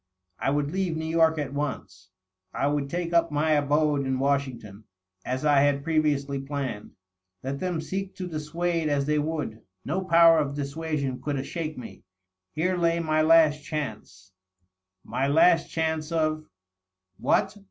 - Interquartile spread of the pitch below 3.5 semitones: Yes, average, 2.7 semitones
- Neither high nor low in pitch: Yes, medium, 150 Hz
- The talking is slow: No, average, 155 wpm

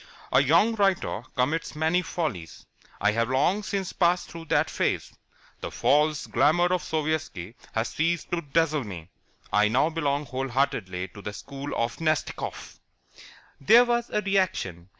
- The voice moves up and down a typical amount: No, wide, 6.7 semitones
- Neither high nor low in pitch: Yes, medium, 150 Hz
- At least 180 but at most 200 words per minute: No, average, 150 wpm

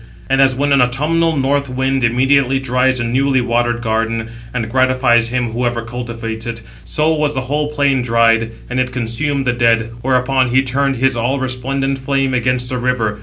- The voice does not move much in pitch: Yes, narrow, 2.3 semitones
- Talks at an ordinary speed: Yes, average, 180 wpm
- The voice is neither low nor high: No, low, 125 Hz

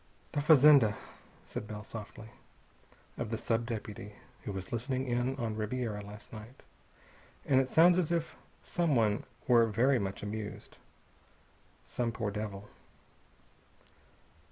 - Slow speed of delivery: Yes, slow, 125 wpm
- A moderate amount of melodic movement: Yes, average, 3.8 semitones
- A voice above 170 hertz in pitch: No, low, 115 Hz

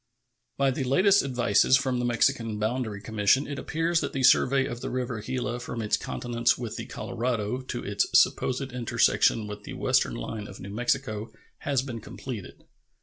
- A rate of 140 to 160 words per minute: No, average, 175 wpm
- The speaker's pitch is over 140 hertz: No, low, 120 Hz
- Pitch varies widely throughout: No, average, 3.3 semitones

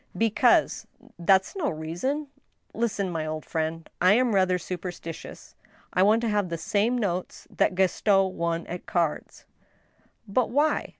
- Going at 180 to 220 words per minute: No, average, 170 wpm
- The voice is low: No, high, 190 Hz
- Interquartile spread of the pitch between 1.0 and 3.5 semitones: No, average, 4.6 semitones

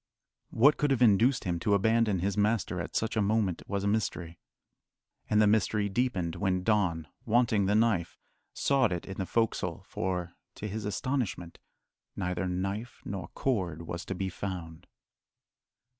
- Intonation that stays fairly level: No, average, 3.7 semitones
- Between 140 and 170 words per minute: Yes, average, 160 wpm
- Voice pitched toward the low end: Yes, low, 100 Hz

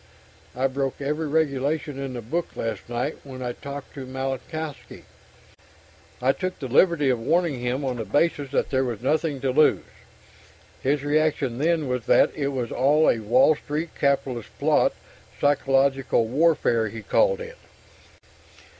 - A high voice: No, low, 135 Hz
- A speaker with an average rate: Yes, average, 155 wpm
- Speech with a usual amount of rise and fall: Yes, average, 3.1 semitones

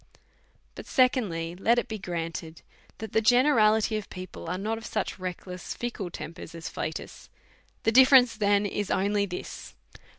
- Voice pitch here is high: Yes, high, 205 Hz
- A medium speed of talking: Yes, average, 155 wpm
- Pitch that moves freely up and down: No, average, 3.8 semitones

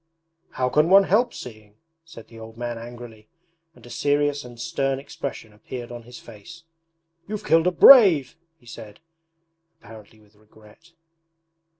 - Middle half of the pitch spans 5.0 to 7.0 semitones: Yes, average, 5.3 semitones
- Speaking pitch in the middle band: No, low, 120 Hz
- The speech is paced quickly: No, average, 145 wpm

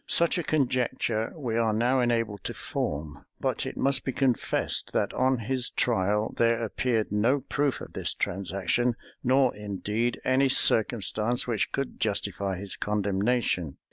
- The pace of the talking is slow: No, average, 145 wpm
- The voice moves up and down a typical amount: Yes, average, 3.8 semitones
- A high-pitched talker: No, low, 115 Hz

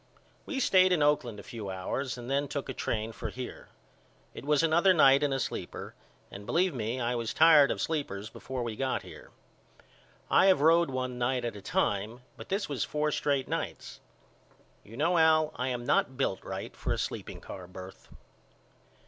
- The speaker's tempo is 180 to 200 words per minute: Yes, average, 190 wpm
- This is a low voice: Yes, low, 130 Hz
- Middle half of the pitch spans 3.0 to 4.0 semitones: No, average, 4.6 semitones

